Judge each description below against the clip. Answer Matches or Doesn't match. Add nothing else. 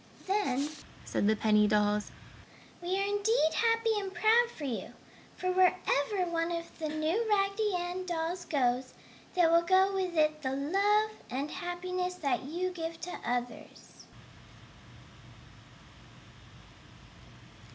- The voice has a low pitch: Doesn't match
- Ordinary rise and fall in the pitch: Matches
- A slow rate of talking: Matches